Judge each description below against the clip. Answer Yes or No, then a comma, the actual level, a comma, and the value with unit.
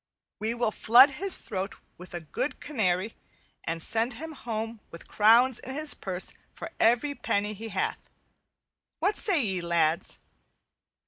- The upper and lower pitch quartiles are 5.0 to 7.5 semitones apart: Yes, wide, 5.6 semitones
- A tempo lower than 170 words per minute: Yes, average, 140 wpm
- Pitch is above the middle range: Yes, high, 225 Hz